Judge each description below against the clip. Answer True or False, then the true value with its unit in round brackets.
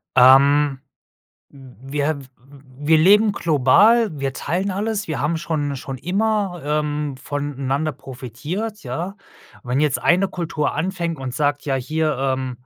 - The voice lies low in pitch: False (145 Hz)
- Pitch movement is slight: False (4.3 semitones)